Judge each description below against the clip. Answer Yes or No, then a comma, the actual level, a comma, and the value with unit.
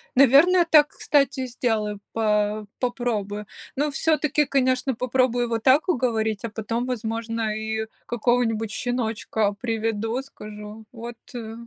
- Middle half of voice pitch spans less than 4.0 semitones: Yes, average, 2.8 semitones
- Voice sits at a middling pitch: No, high, 230 Hz